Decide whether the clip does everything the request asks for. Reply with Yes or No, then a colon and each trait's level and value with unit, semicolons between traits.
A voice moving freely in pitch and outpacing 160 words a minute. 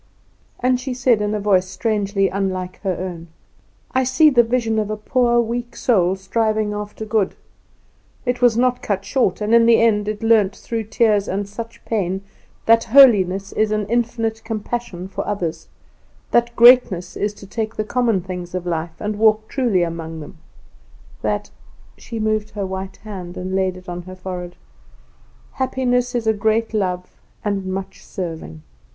No: average, 3.6 semitones; average, 170 wpm